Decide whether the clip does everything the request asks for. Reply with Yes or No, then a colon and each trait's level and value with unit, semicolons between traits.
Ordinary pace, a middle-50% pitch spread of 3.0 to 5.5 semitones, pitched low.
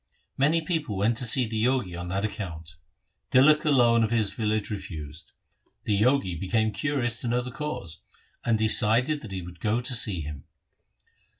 Yes: average, 175 wpm; average, 4.8 semitones; low, 110 Hz